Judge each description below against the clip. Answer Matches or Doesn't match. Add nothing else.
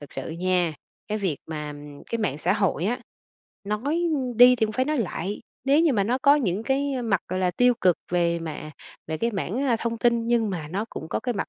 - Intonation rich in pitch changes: Matches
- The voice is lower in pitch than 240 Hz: Matches